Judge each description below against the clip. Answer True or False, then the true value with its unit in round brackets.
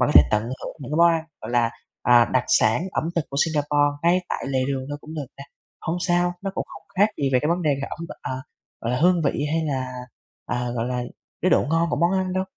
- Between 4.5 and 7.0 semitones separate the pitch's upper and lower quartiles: True (4.9 semitones)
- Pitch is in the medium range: True (145 Hz)